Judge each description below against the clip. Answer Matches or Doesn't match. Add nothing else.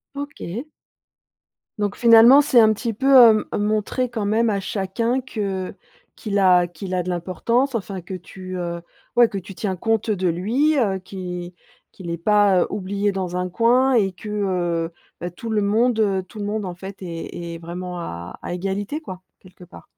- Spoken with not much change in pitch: Doesn't match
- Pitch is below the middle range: Doesn't match